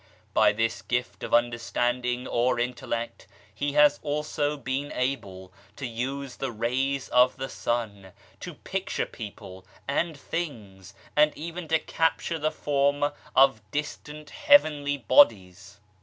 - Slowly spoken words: Yes, slow, 125 wpm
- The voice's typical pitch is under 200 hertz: Yes, low, 135 Hz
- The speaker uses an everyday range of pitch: Yes, average, 3.8 semitones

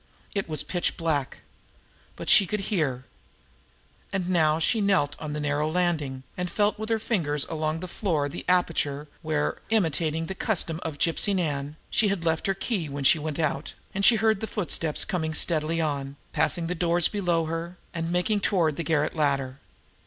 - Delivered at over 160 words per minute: Yes, average, 185 wpm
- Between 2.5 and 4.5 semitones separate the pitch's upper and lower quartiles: Yes, average, 3.5 semitones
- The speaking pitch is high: No, medium, 165 Hz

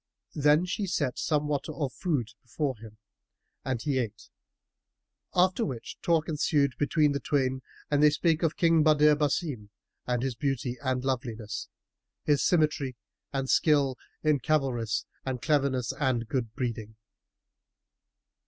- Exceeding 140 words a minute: No, slow, 135 wpm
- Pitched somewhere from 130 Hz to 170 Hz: Yes, medium, 140 Hz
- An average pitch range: Yes, average, 3.3 semitones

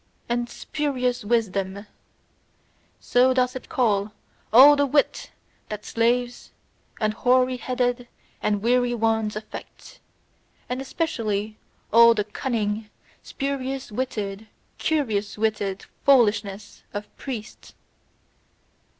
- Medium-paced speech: No, slow, 100 wpm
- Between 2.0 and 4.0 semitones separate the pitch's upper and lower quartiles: Yes, average, 3.3 semitones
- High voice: Yes, high, 235 Hz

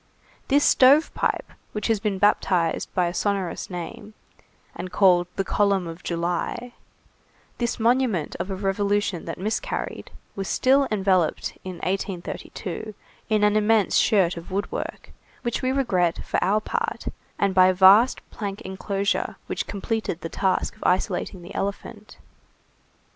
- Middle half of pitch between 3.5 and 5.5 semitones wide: No, average, 2.8 semitones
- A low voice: No, high, 200 Hz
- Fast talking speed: No, average, 145 wpm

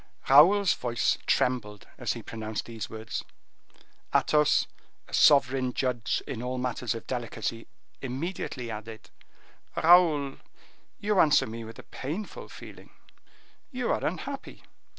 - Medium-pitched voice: No, low, 125 Hz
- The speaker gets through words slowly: Yes, slow, 120 wpm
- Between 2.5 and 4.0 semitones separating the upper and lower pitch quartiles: No, average, 4.7 semitones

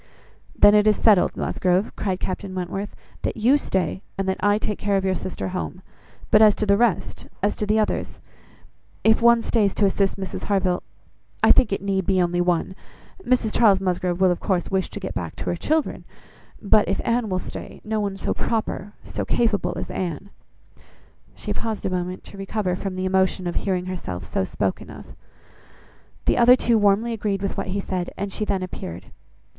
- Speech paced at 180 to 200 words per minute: Yes, average, 195 wpm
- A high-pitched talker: Yes, high, 195 Hz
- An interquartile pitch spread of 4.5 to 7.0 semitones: No, narrow, 2.4 semitones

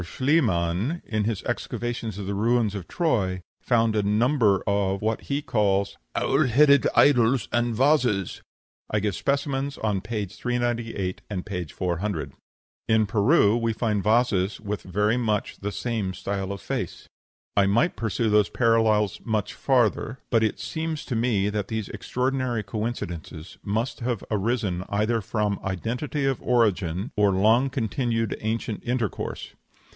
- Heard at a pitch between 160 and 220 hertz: No, low, 110 Hz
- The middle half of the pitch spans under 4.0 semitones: Yes, average, 3.3 semitones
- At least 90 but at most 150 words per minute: Yes, average, 145 wpm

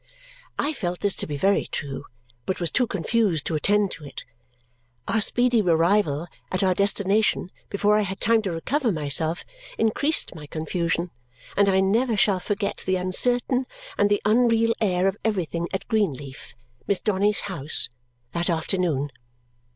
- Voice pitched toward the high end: Yes, high, 195 Hz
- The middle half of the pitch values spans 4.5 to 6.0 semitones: No, average, 4.1 semitones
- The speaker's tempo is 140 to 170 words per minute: Yes, average, 155 wpm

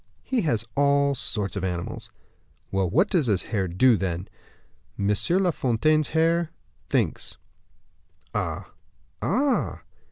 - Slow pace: Yes, slow, 120 wpm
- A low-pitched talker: Yes, low, 130 Hz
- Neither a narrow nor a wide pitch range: No, wide, 8.7 semitones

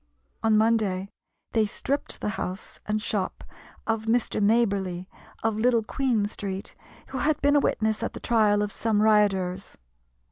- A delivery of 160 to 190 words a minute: No, average, 150 wpm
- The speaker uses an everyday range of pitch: No, narrow, 2.0 semitones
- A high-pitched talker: Yes, high, 215 Hz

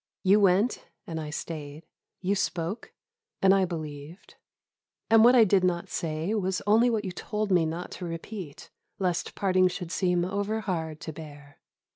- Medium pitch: Yes, medium, 180 Hz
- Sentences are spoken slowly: No, average, 165 wpm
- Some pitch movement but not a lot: Yes, average, 3.8 semitones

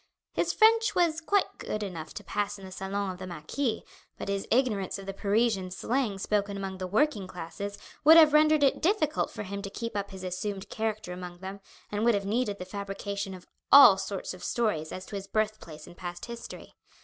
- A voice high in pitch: Yes, high, 200 Hz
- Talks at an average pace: No, fast, 210 wpm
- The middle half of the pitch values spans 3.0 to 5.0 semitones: Yes, average, 3.7 semitones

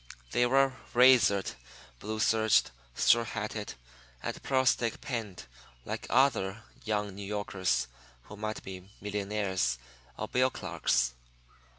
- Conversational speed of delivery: No, slow, 115 wpm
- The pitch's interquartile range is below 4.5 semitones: Yes, average, 3.5 semitones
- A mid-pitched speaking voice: No, low, 105 Hz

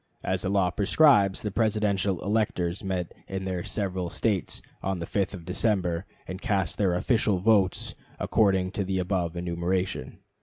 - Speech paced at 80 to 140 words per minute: No, average, 155 wpm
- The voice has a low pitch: Yes, very low, 95 Hz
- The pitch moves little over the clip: Yes, narrow, 2.2 semitones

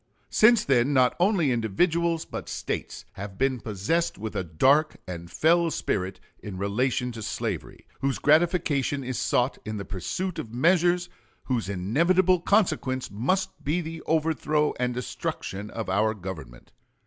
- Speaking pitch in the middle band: No, low, 130 Hz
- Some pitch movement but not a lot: No, wide, 7.8 semitones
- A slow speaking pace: No, average, 145 wpm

